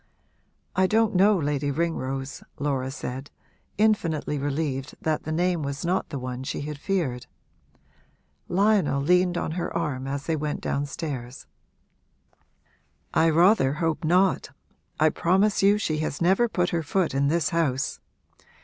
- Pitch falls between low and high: Yes, medium, 155 Hz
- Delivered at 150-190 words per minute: No, average, 140 wpm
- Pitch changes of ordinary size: Yes, average, 4.3 semitones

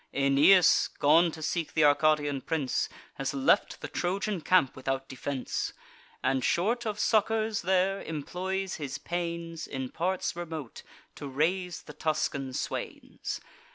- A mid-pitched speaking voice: Yes, medium, 160 Hz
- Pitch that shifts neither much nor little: Yes, average, 4.7 semitones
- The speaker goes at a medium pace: No, slow, 130 wpm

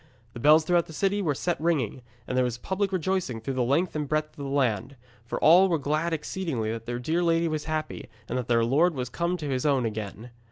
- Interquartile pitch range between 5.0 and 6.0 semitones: Yes, average, 5.3 semitones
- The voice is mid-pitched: Yes, medium, 150 Hz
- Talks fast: Yes, fast, 240 wpm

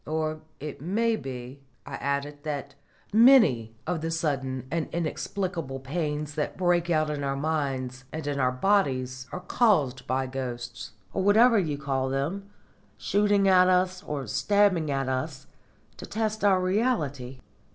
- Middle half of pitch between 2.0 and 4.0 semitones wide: No, wide, 5.6 semitones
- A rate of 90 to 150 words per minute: Yes, average, 145 wpm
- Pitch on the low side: No, medium, 150 Hz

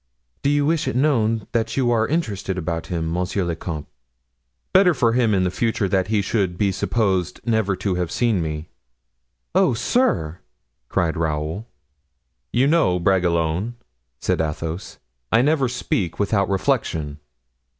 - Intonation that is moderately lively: No, wide, 5.7 semitones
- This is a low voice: Yes, low, 100 Hz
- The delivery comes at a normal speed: Yes, average, 145 wpm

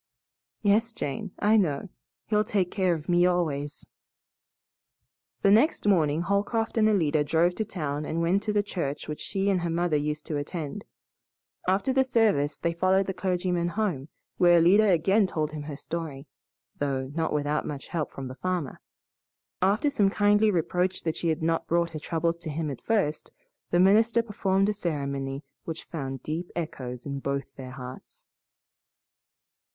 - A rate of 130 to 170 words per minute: Yes, average, 165 wpm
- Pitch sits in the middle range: Yes, medium, 170 Hz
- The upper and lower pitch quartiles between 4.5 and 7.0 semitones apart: Yes, average, 4.9 semitones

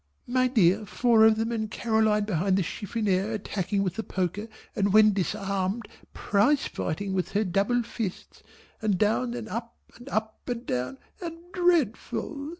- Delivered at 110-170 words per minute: Yes, average, 155 wpm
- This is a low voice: No, high, 215 Hz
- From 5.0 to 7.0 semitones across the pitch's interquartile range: No, average, 3.2 semitones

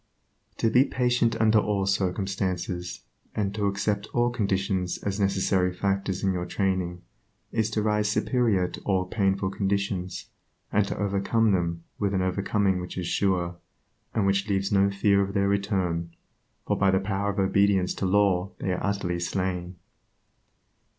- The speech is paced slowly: No, average, 155 wpm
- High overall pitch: No, low, 100 Hz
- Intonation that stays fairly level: Yes, narrow, 1.7 semitones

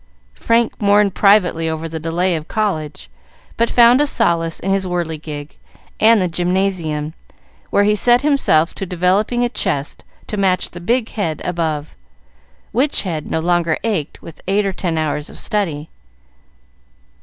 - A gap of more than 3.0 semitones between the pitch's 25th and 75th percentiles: Yes, average, 4.5 semitones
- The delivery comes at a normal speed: Yes, average, 155 wpm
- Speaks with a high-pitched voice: No, medium, 180 Hz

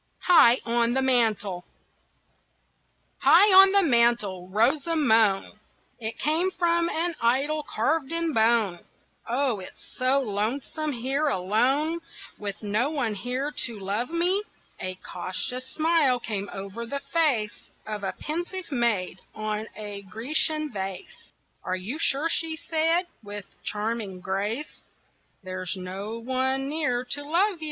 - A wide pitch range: Yes, wide, 6.7 semitones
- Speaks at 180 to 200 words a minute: No, slow, 135 wpm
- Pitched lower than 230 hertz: No, high, 245 Hz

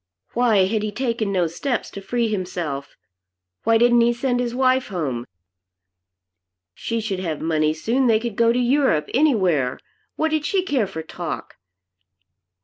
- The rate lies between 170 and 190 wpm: No, average, 155 wpm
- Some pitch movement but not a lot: No, wide, 5.8 semitones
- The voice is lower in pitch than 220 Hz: No, high, 225 Hz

